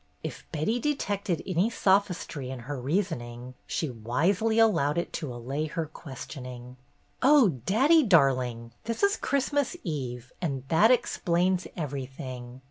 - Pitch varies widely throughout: Yes, wide, 7.9 semitones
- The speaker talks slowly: Yes, slow, 125 wpm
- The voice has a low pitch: No, medium, 155 Hz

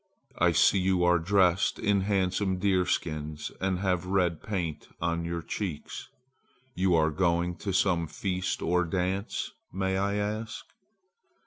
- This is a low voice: Yes, very low, 90 Hz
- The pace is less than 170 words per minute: Yes, slow, 135 wpm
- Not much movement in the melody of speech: Yes, narrow, 2.2 semitones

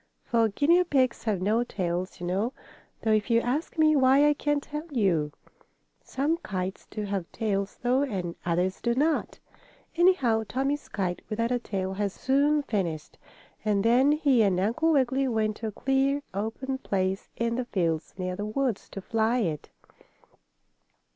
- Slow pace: No, average, 165 wpm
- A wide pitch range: Yes, wide, 5.8 semitones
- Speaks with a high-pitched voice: Yes, high, 230 Hz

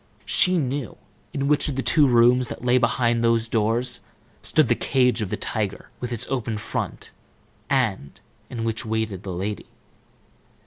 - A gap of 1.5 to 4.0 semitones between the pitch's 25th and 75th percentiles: Yes, narrow, 2.6 semitones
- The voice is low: Yes, low, 120 Hz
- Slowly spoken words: No, average, 165 wpm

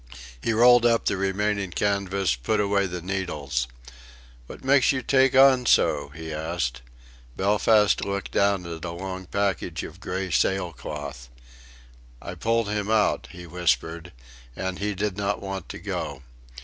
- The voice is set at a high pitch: No, very low, 95 Hz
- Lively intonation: No, average, 3.5 semitones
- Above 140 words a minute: Yes, average, 150 wpm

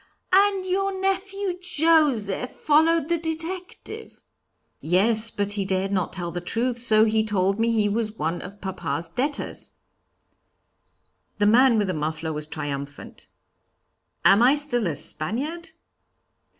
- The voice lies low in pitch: No, high, 225 Hz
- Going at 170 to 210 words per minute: No, slow, 135 wpm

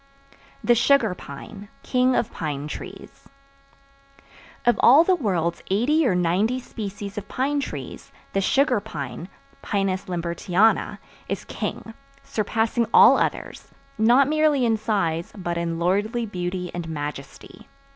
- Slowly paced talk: Yes, slow, 125 wpm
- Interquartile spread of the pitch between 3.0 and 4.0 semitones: No, wide, 5.6 semitones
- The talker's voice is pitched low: No, high, 205 Hz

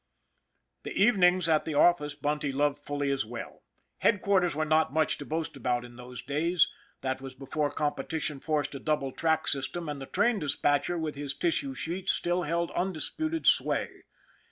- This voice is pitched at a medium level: Yes, medium, 150 Hz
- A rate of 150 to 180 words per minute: Yes, average, 170 wpm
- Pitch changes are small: No, average, 3.5 semitones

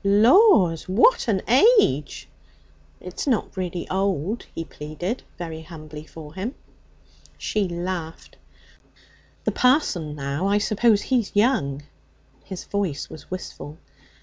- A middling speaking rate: No, slow, 115 wpm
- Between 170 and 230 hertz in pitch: Yes, medium, 185 Hz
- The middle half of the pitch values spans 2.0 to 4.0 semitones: No, average, 5.1 semitones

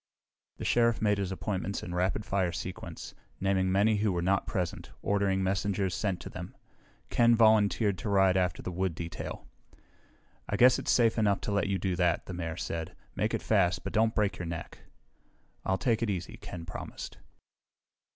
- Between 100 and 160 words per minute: No, average, 180 wpm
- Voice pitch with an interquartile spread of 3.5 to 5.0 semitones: No, narrow, 2.6 semitones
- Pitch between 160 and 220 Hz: No, very low, 95 Hz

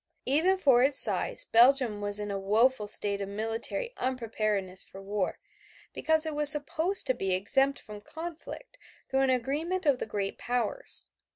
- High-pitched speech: Yes, very high, 250 Hz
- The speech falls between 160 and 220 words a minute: Yes, average, 165 wpm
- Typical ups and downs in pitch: No, wide, 6.3 semitones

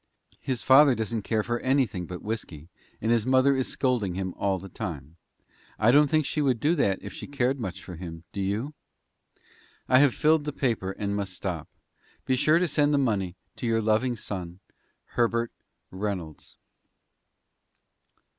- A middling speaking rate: Yes, average, 170 wpm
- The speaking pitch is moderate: No, low, 115 Hz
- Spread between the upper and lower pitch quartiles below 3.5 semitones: No, wide, 5.6 semitones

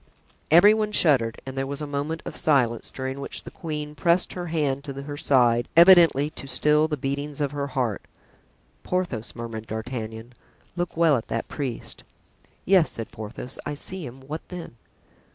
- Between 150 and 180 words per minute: Yes, average, 170 wpm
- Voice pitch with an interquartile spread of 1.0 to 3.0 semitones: No, average, 4.3 semitones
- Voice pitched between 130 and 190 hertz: Yes, medium, 140 Hz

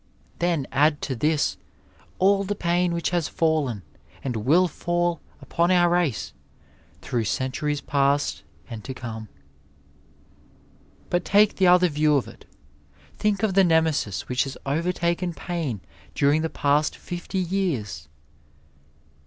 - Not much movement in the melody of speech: No, average, 4.5 semitones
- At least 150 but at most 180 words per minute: No, slow, 135 wpm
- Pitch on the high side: No, medium, 160 Hz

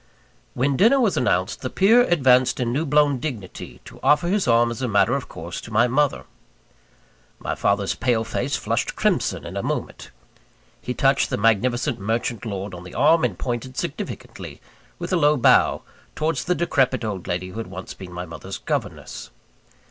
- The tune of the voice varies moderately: No, wide, 6.1 semitones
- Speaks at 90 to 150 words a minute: No, average, 180 wpm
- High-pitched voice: No, low, 125 Hz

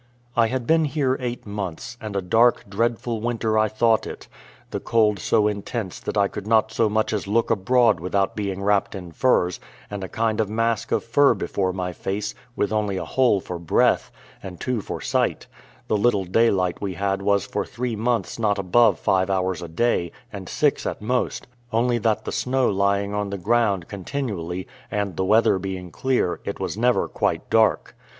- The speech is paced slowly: No, average, 190 wpm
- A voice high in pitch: No, low, 105 Hz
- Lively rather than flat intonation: No, average, 3.2 semitones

